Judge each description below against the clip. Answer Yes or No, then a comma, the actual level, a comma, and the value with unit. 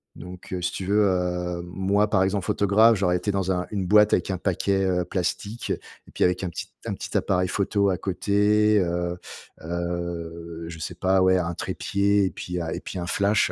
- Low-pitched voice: Yes, very low, 95 Hz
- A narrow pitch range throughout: Yes, narrow, 2.3 semitones